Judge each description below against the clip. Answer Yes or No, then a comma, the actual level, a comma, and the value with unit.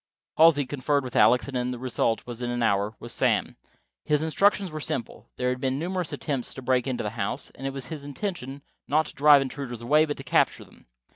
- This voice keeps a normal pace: No, fast, 210 wpm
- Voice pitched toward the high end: No, low, 135 Hz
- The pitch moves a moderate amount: Yes, average, 3.3 semitones